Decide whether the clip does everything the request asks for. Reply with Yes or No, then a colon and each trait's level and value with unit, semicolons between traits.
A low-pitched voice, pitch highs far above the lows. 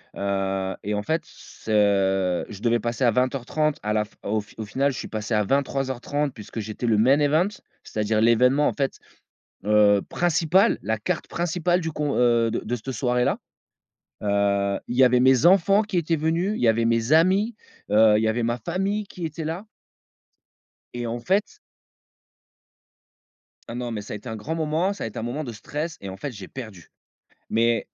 Yes: low, 120 Hz; wide, 6.3 semitones